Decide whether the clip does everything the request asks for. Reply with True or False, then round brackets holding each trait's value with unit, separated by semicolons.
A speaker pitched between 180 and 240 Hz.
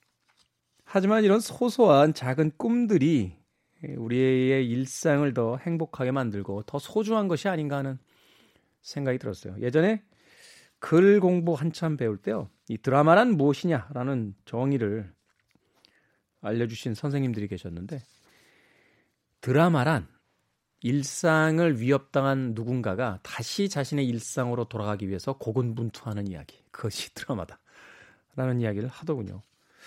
False (135 Hz)